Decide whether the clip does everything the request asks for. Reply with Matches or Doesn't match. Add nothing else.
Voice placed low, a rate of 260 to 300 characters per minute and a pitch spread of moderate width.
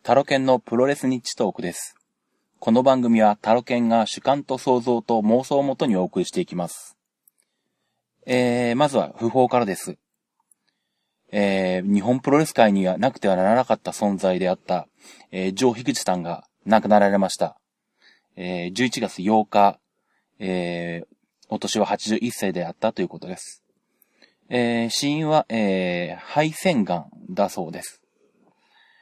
Matches